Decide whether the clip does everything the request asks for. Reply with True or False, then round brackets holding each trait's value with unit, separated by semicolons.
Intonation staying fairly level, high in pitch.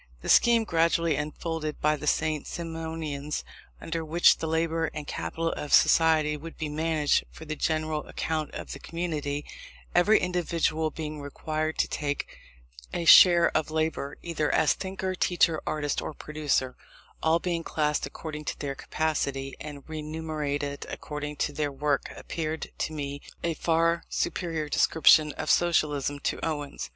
False (1.7 semitones; 155 Hz)